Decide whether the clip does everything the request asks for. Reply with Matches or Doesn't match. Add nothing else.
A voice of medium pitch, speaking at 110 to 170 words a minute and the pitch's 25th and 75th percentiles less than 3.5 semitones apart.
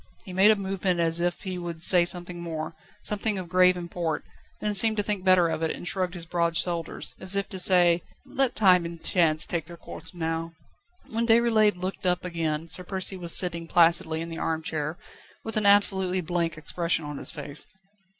Doesn't match